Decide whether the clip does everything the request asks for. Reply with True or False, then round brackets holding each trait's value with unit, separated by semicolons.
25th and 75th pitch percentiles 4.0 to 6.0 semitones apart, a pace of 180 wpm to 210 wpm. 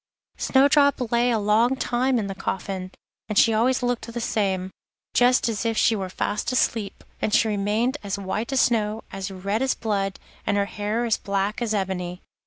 False (3.3 semitones; 190 wpm)